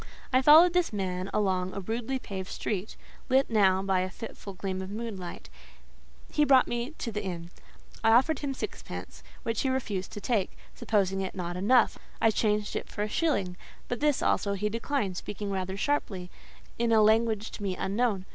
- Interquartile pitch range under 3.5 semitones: No, average, 4.1 semitones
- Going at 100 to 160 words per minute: No, average, 185 wpm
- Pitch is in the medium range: No, high, 210 Hz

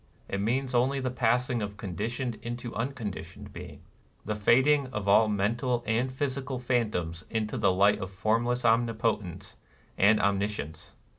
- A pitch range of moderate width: Yes, average, 3.4 semitones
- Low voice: Yes, low, 115 Hz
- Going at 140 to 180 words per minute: Yes, average, 155 wpm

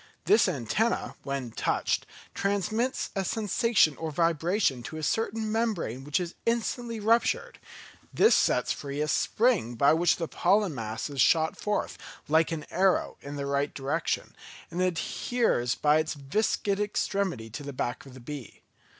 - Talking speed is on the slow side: No, average, 155 wpm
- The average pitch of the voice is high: No, medium, 165 Hz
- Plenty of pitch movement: Yes, wide, 6.8 semitones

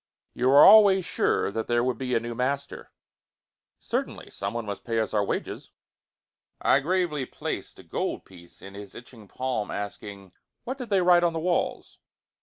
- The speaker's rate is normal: Yes, average, 175 wpm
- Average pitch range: No, wide, 8.5 semitones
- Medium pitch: No, low, 125 Hz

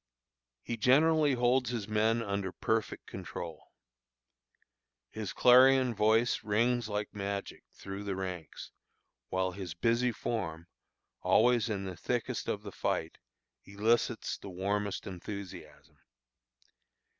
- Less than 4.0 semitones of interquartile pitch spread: Yes, average, 3.5 semitones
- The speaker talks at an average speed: No, slow, 110 wpm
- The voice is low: Yes, low, 105 Hz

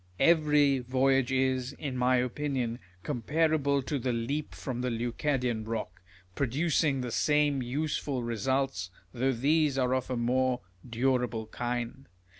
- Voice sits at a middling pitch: No, low, 130 Hz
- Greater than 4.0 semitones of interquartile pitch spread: No, narrow, 2.6 semitones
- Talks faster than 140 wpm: No, slow, 135 wpm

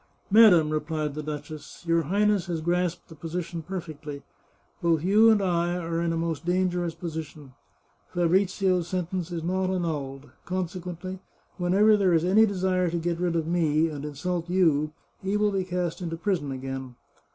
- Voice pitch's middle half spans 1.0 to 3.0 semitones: Yes, narrow, 2.5 semitones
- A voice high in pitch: No, medium, 175 Hz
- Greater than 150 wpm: Yes, average, 170 wpm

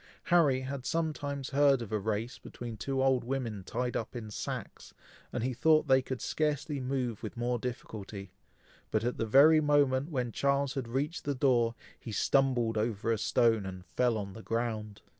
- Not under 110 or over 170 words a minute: No, average, 180 wpm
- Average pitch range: Yes, average, 3.6 semitones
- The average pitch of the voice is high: No, low, 125 Hz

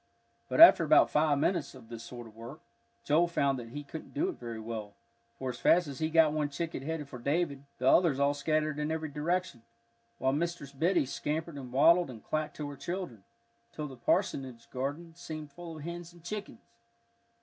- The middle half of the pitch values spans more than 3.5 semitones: Yes, average, 4.0 semitones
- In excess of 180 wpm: Yes, average, 200 wpm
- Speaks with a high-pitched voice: No, medium, 150 Hz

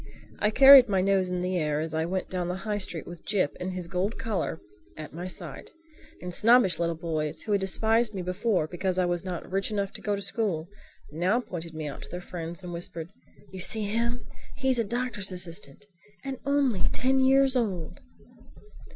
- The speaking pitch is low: No, medium, 185 Hz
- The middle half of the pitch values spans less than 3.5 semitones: No, average, 4.2 semitones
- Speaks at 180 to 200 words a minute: Yes, average, 195 wpm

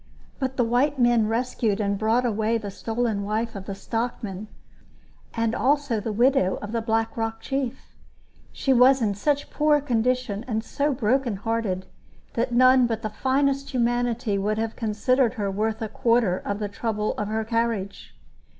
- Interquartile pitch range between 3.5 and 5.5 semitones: No, average, 2.9 semitones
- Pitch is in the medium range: No, high, 230 Hz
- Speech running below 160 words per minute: No, average, 170 wpm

